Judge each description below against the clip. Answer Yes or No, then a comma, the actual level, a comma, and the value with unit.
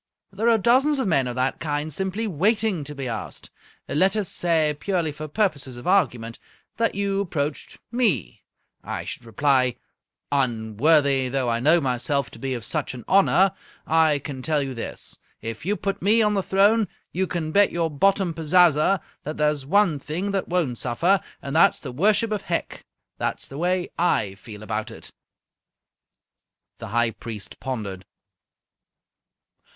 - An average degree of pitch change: No, wide, 7.0 semitones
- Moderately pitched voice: Yes, medium, 155 Hz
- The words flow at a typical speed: Yes, average, 165 wpm